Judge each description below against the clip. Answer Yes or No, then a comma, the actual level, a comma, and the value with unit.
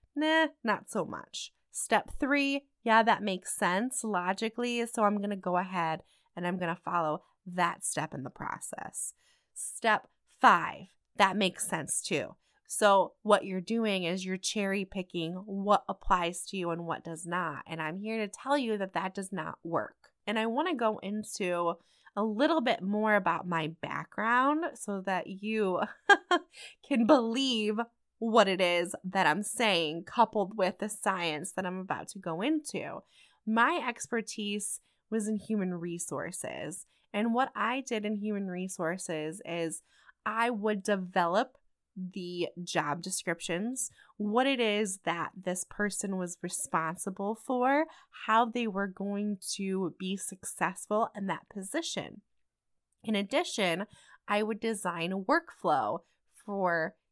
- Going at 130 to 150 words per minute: Yes, average, 145 wpm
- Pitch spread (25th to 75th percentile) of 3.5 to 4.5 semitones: Yes, average, 4.1 semitones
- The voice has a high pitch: Yes, high, 200 Hz